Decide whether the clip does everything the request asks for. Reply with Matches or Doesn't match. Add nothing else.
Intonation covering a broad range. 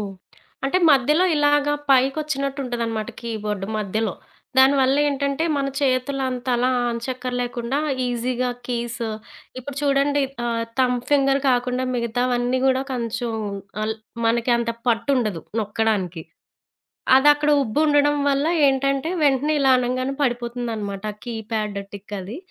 Doesn't match